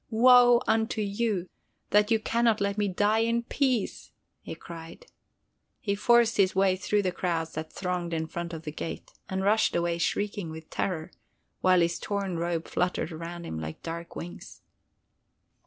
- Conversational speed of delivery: Yes, average, 170 wpm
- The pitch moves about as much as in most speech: Yes, average, 4.0 semitones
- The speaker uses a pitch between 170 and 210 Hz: Yes, medium, 185 Hz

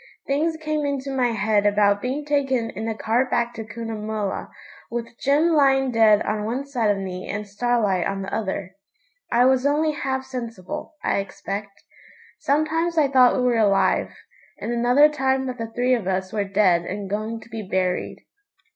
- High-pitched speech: Yes, high, 230 Hz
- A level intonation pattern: No, average, 4.6 semitones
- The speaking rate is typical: Yes, average, 180 wpm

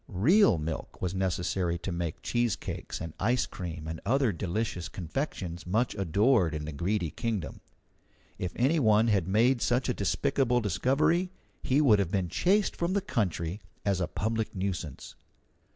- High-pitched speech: No, low, 100 Hz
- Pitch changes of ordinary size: No, wide, 5.9 semitones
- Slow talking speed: No, average, 155 wpm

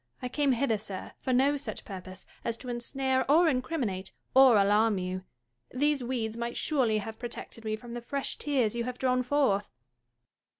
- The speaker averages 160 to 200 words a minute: Yes, average, 175 wpm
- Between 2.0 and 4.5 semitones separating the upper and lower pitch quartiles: Yes, average, 3.6 semitones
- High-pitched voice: Yes, high, 240 Hz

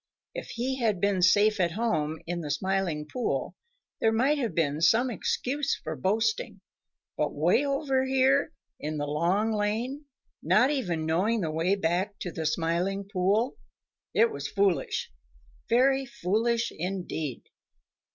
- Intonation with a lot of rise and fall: Yes, wide, 6.3 semitones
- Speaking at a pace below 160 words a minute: Yes, average, 140 wpm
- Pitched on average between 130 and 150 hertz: No, high, 205 Hz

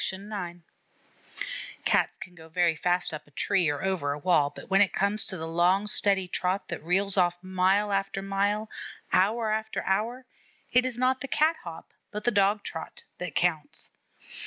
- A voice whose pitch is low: No, high, 190 Hz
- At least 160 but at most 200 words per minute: Yes, average, 185 wpm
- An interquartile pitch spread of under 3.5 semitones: Yes, average, 3.0 semitones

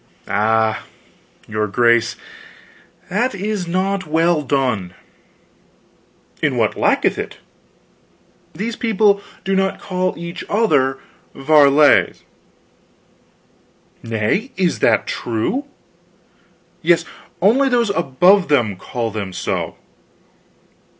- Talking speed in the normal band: No, slow, 90 wpm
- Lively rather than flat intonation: Yes, wide, 8.9 semitones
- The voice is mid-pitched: Yes, medium, 165 Hz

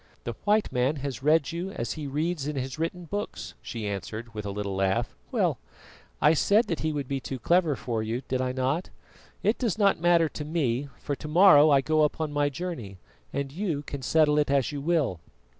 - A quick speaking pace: Yes, fast, 210 wpm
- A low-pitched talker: No, medium, 145 Hz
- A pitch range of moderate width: Yes, average, 4.4 semitones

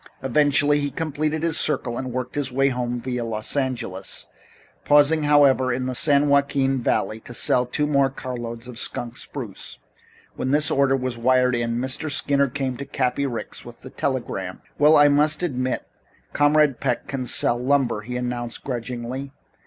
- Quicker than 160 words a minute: Yes, average, 170 wpm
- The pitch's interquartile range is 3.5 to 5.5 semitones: No, average, 2.7 semitones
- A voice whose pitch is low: Yes, low, 130 Hz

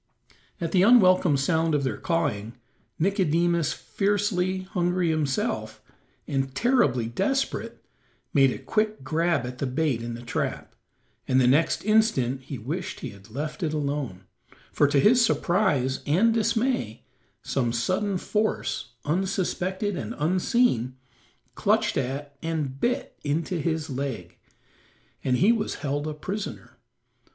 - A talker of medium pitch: Yes, medium, 160 Hz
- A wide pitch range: Yes, wide, 6.0 semitones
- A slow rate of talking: Yes, slow, 130 wpm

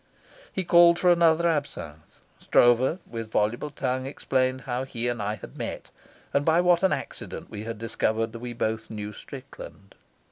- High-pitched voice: No, low, 125 Hz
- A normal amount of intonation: No, wide, 6.1 semitones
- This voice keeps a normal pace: Yes, average, 165 wpm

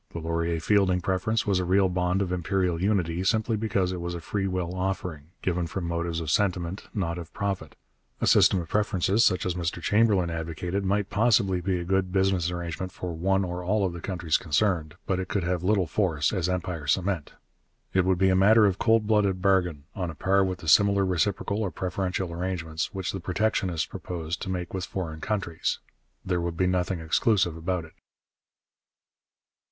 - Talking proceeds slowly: No, average, 190 wpm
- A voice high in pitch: No, very low, 90 Hz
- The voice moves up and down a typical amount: No, narrow, 2.3 semitones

